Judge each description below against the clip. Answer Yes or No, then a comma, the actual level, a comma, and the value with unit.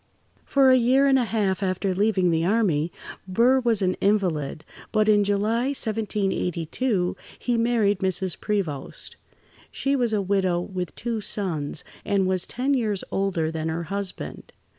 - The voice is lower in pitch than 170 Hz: No, high, 200 Hz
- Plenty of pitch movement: No, average, 4.0 semitones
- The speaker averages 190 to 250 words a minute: No, average, 155 wpm